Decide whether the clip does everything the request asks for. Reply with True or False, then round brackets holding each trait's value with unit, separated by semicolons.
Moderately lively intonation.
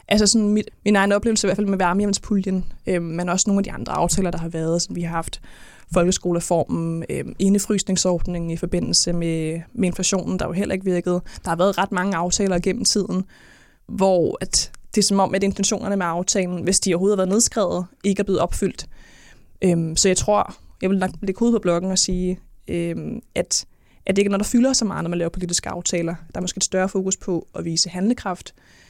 False (2.3 semitones)